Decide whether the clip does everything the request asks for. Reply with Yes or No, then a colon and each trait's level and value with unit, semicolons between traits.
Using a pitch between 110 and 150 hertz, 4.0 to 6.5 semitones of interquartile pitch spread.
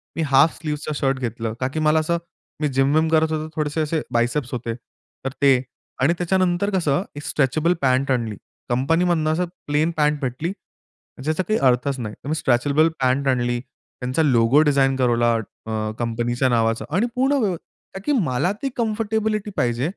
Yes: medium, 140 Hz; average, 4.5 semitones